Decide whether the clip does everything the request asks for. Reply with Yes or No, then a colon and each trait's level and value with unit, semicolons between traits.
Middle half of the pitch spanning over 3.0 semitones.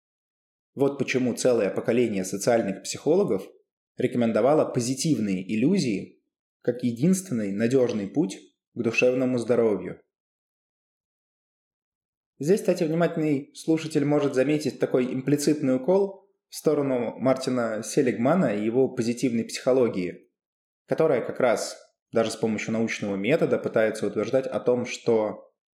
Yes: average, 4.3 semitones